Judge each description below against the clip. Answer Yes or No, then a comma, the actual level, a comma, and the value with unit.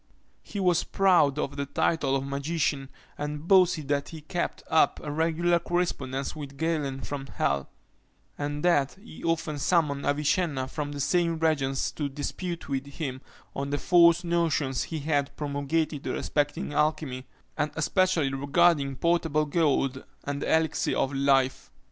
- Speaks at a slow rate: No, average, 150 wpm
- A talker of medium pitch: Yes, medium, 150 Hz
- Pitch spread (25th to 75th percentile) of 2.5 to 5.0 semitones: Yes, average, 3.1 semitones